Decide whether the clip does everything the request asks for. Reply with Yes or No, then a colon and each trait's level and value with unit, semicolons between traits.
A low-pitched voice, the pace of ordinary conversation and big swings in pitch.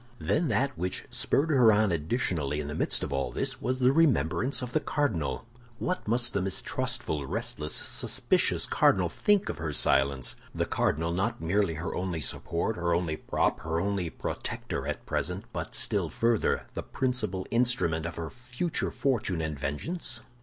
Yes: very low, 95 Hz; average, 165 wpm; wide, 7.6 semitones